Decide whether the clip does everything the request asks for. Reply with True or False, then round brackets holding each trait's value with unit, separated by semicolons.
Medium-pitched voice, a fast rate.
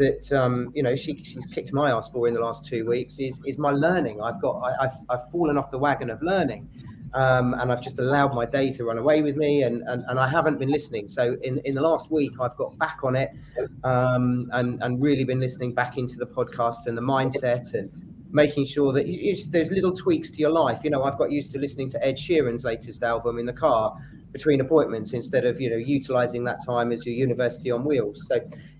False (130 Hz; 235 wpm)